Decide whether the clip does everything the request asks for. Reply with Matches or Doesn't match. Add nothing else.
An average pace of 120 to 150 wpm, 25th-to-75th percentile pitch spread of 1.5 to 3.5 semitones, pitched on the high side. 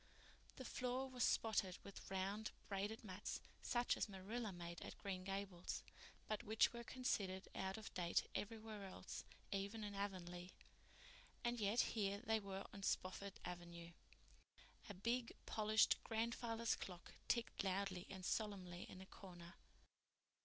Matches